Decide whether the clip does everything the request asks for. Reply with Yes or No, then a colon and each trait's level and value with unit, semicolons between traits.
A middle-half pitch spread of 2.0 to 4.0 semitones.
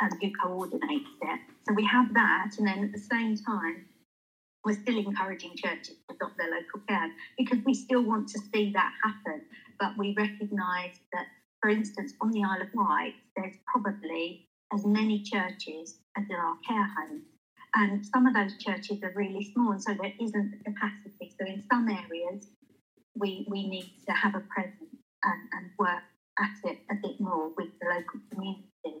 Yes: average, 2.9 semitones